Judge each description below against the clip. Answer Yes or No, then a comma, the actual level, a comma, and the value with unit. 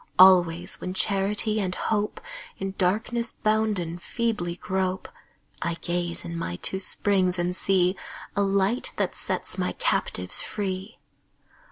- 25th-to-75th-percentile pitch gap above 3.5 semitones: No, average, 2.7 semitones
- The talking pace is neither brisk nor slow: No, slow, 130 wpm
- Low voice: No, high, 190 Hz